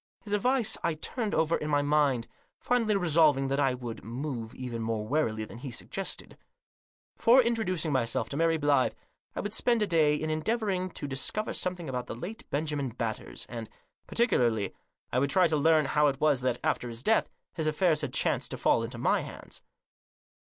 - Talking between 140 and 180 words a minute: No, average, 190 wpm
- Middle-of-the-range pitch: Yes, medium, 150 Hz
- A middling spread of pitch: No, wide, 6.3 semitones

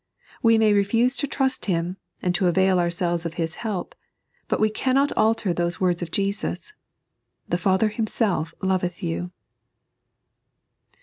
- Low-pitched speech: No, high, 190 Hz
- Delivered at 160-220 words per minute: No, average, 145 wpm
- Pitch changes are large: No, average, 4.1 semitones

